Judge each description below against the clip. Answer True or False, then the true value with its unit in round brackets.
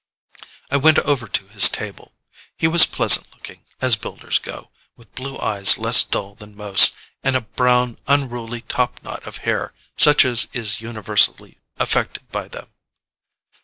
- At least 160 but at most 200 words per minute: False (150 wpm)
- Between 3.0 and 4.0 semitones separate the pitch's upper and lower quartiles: True (3.5 semitones)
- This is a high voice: False (120 Hz)